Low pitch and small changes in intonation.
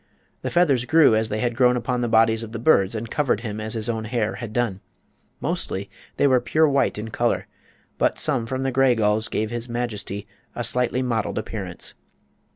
Yes: low, 115 Hz; narrow, 2.3 semitones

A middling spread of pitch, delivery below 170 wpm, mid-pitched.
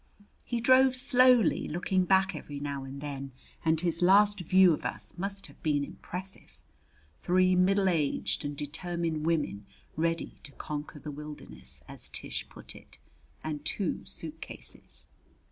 Yes: average, 4.4 semitones; average, 145 wpm; medium, 165 Hz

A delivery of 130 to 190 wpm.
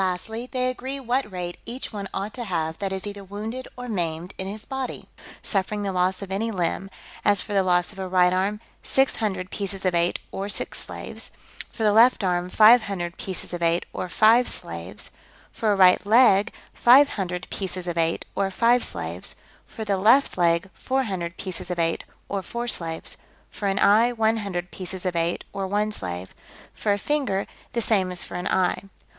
No: average, 200 wpm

